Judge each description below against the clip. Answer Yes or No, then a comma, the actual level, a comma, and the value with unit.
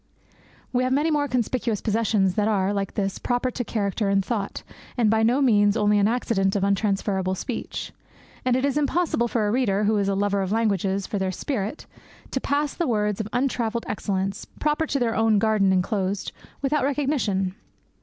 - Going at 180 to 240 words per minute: Yes, average, 185 wpm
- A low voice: No, high, 215 Hz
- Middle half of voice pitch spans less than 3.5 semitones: No, average, 4.2 semitones